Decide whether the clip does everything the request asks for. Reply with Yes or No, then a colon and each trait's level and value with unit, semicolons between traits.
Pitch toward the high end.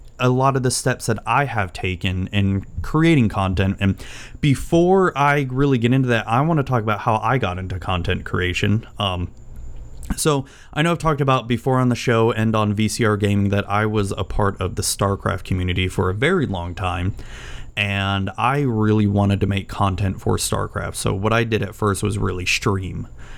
No: low, 105 Hz